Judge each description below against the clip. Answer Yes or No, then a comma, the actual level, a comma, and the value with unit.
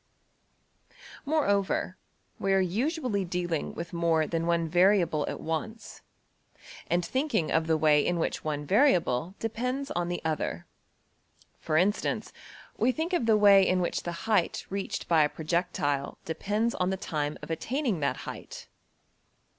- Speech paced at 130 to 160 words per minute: Yes, average, 145 wpm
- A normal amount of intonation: Yes, average, 4.7 semitones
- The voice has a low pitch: No, medium, 180 Hz